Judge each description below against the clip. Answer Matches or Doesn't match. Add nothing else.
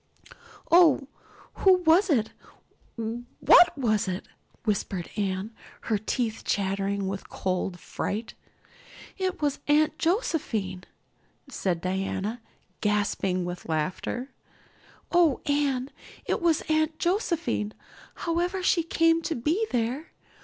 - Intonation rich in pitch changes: Matches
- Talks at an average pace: Doesn't match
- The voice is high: Matches